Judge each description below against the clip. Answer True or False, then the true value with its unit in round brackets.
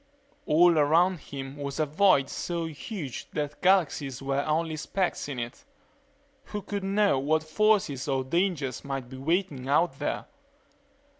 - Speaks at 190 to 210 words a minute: False (145 wpm)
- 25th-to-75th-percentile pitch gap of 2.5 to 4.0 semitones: False (4.7 semitones)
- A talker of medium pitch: True (155 Hz)